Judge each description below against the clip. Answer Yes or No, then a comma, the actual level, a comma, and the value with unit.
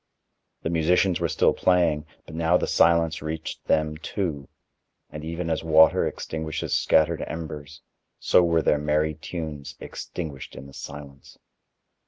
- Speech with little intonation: Yes, narrow, 1.8 semitones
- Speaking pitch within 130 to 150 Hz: No, very low, 80 Hz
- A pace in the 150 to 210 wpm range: No, average, 140 wpm